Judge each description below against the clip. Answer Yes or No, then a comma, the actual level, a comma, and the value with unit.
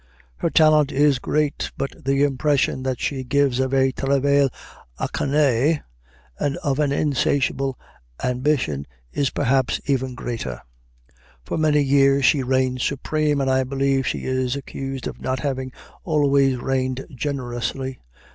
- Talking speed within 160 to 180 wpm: No, slow, 135 wpm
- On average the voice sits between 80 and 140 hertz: Yes, low, 135 Hz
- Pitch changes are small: Yes, narrow, 1.5 semitones